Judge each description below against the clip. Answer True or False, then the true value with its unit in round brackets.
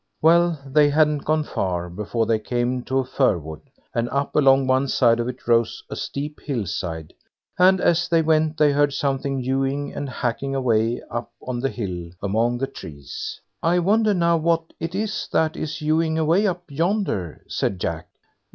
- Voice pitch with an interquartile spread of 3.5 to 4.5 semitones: False (5.3 semitones)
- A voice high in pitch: False (135 Hz)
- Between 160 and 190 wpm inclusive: True (180 wpm)